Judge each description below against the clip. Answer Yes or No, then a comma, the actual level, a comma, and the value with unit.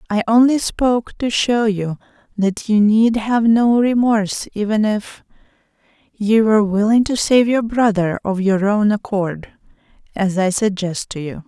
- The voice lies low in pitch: No, high, 215 Hz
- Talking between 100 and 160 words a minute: Yes, average, 155 wpm